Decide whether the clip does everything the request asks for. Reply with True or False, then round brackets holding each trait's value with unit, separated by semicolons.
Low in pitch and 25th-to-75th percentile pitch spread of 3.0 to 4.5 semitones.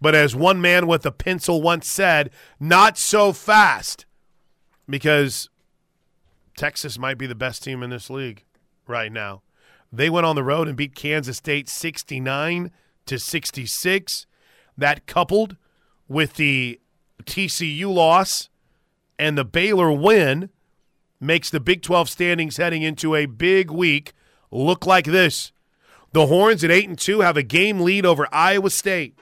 False (165 Hz; 4.1 semitones)